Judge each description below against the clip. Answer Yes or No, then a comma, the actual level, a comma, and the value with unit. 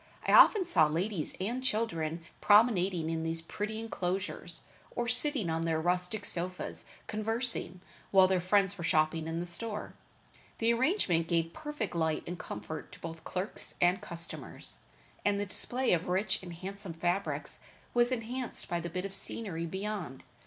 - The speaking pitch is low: No, medium, 185 Hz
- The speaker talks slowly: No, average, 160 wpm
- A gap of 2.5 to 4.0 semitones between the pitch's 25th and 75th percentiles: No, average, 4.5 semitones